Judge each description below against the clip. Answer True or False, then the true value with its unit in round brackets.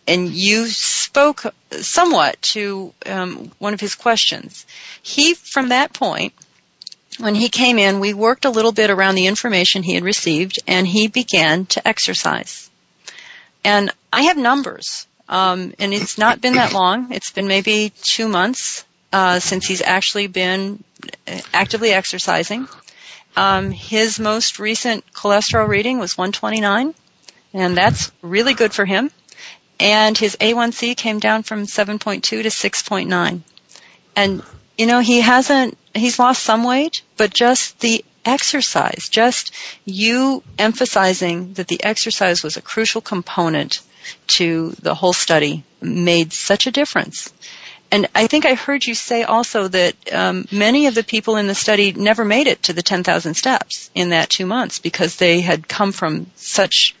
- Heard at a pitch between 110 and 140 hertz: False (215 Hz)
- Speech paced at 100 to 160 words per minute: True (155 wpm)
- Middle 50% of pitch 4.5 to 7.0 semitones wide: False (4.1 semitones)